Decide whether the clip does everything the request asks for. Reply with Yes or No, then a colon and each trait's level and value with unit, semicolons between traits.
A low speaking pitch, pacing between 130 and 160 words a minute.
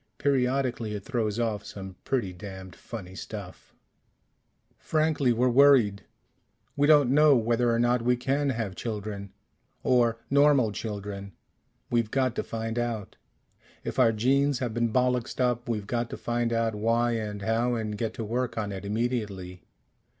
Yes: low, 115 Hz; average, 155 wpm